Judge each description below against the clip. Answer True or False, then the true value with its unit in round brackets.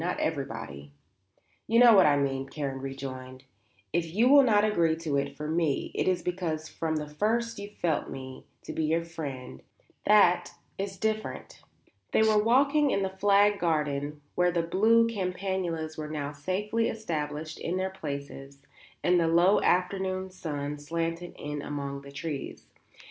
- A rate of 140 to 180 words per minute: True (160 wpm)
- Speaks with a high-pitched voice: False (165 Hz)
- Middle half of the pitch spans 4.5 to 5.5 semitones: True (5.1 semitones)